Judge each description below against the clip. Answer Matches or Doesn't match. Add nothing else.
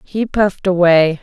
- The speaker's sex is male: Doesn't match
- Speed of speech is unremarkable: Matches